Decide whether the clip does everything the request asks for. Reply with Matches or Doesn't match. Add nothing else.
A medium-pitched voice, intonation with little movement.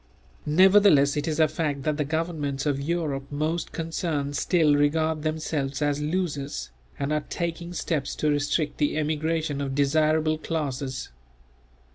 Matches